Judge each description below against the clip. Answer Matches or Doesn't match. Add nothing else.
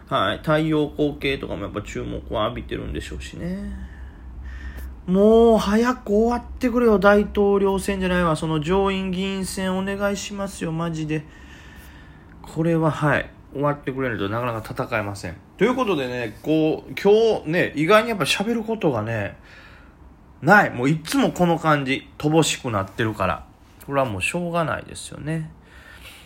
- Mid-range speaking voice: Matches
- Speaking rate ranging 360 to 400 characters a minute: Doesn't match